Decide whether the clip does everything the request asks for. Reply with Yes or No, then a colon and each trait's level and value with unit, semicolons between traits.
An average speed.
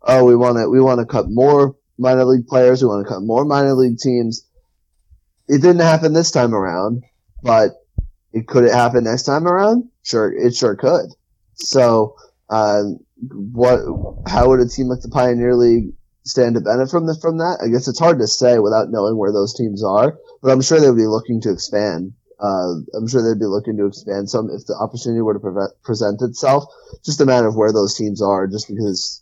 No: fast, 215 wpm